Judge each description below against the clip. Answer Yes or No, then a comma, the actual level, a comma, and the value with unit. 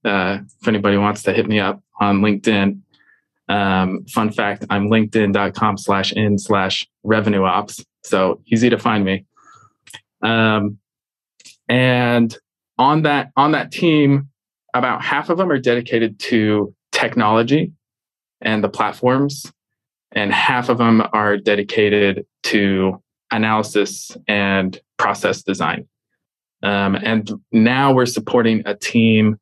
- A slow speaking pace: Yes, slow, 115 wpm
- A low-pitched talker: Yes, low, 110 Hz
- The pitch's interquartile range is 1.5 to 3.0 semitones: Yes, narrow, 2.5 semitones